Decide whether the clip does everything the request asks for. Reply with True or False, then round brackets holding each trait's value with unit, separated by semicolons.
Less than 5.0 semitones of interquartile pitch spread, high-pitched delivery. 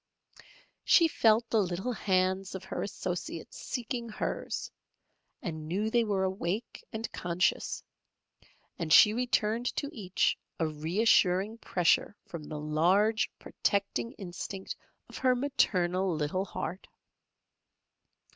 True (4.1 semitones; 195 Hz)